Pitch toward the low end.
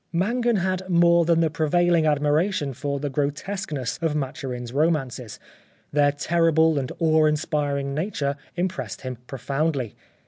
No: medium, 150 Hz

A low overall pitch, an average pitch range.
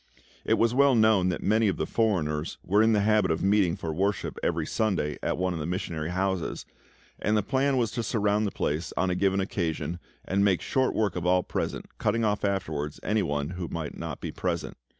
Yes: very low, 95 Hz; average, 4.0 semitones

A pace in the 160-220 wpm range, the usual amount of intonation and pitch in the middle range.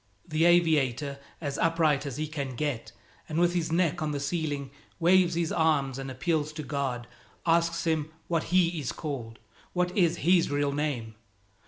Yes: average, 170 wpm; average, 3.2 semitones; medium, 155 Hz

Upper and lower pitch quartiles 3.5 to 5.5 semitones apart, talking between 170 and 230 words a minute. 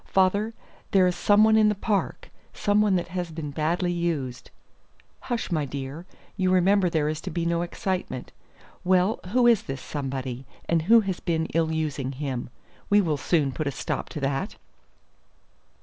Yes: average, 4.6 semitones; average, 175 wpm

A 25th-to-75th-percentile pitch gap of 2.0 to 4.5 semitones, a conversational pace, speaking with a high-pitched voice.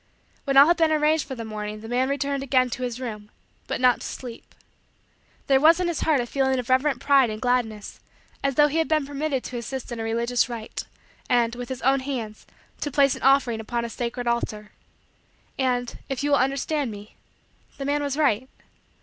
No: average, 3.0 semitones; fast, 210 wpm; very high, 255 Hz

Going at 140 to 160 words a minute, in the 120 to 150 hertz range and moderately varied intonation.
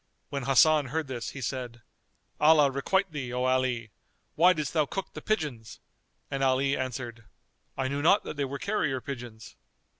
No: average, 170 wpm; low, 135 Hz; average, 3.3 semitones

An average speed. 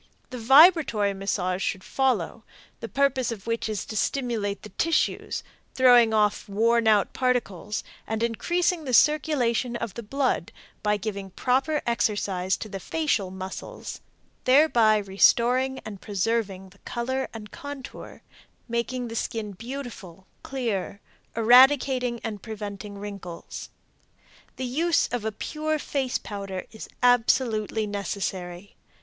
No: slow, 125 wpm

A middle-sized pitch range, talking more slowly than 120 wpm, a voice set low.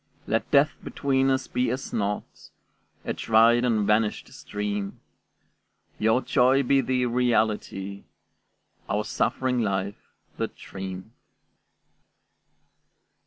Yes: average, 3.6 semitones; slow, 100 wpm; low, 115 Hz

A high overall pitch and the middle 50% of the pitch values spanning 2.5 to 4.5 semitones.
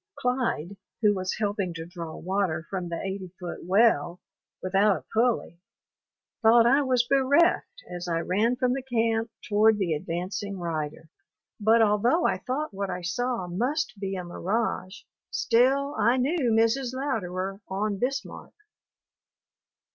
No: high, 210 Hz; average, 5.2 semitones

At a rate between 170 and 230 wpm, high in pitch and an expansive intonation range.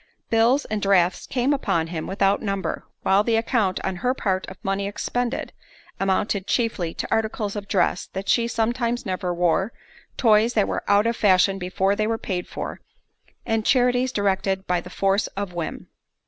No: average, 175 wpm; high, 200 Hz; average, 3.2 semitones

